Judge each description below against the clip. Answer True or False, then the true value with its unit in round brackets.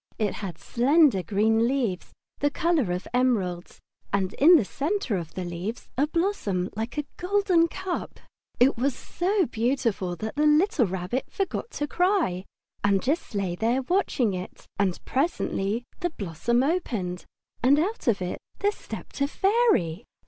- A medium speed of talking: True (155 wpm)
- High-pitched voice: True (245 Hz)